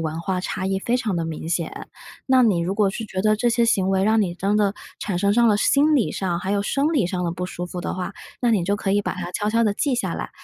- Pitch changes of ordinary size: Yes, average, 3.7 semitones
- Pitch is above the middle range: Yes, high, 200 Hz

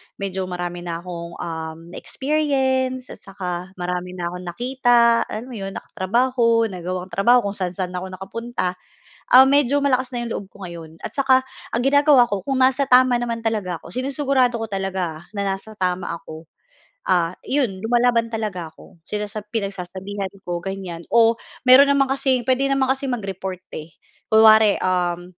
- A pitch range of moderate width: No, wide, 5.9 semitones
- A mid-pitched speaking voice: No, high, 210 Hz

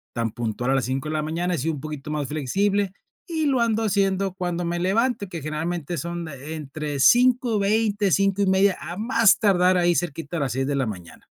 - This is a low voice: No, medium, 175 Hz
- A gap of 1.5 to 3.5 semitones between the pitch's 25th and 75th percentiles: No, wide, 5.4 semitones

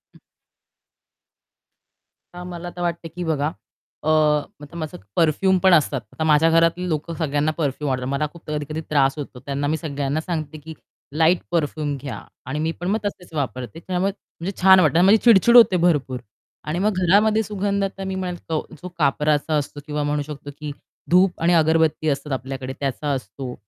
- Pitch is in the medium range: Yes, medium, 155 Hz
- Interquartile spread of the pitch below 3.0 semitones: No, average, 3.5 semitones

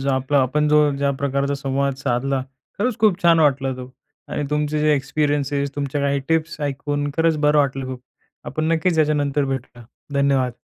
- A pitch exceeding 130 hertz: Yes, medium, 140 Hz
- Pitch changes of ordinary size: No, narrow, 1.9 semitones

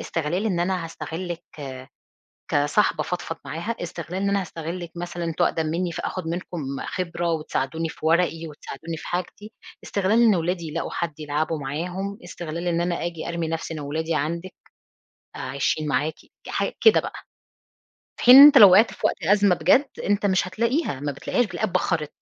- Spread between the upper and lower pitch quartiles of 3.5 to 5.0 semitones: No, average, 2.8 semitones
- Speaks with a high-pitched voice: No, medium, 170 Hz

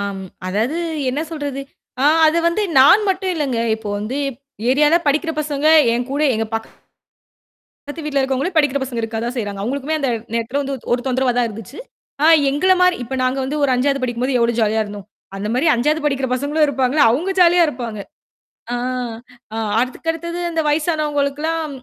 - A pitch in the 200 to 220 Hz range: No, very high, 275 Hz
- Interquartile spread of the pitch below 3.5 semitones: No, average, 4.1 semitones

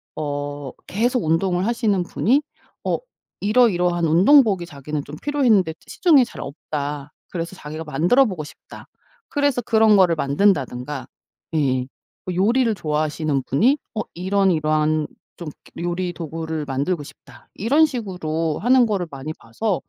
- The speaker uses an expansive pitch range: Yes, wide, 6.2 semitones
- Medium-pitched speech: Yes, medium, 175 Hz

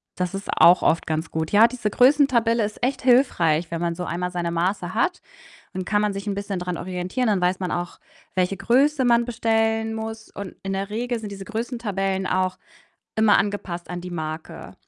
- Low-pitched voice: No, high, 200 Hz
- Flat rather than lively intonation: No, average, 4.1 semitones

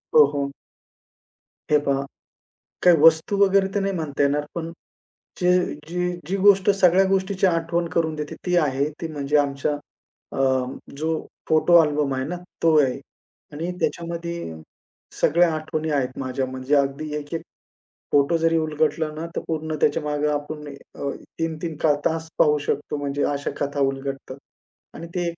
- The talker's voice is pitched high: No, medium, 155 Hz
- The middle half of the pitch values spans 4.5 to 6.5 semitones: No, average, 2.9 semitones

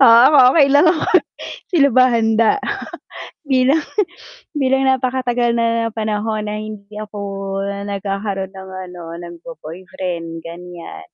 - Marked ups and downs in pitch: No, average, 4.7 semitones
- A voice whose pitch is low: No, high, 220 Hz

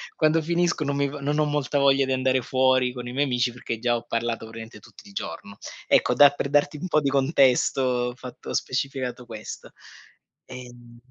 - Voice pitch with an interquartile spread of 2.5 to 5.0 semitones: Yes, average, 2.8 semitones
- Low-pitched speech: Yes, low, 130 Hz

